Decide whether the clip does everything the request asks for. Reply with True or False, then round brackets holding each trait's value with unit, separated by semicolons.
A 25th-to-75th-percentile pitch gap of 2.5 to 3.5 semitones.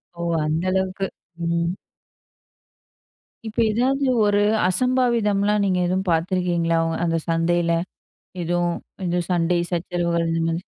True (3.0 semitones)